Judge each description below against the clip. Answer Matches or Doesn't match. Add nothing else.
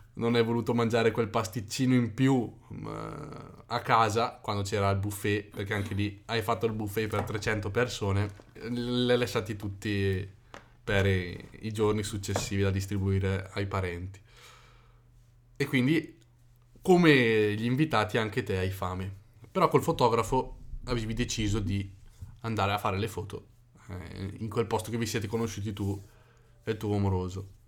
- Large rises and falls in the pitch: Doesn't match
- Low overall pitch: Matches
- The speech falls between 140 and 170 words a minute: Matches